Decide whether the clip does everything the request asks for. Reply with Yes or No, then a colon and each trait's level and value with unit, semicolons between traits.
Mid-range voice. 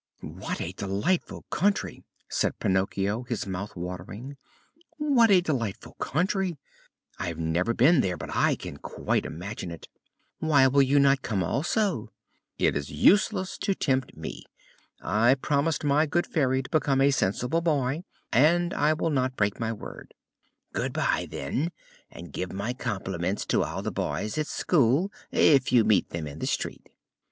No: low, 130 Hz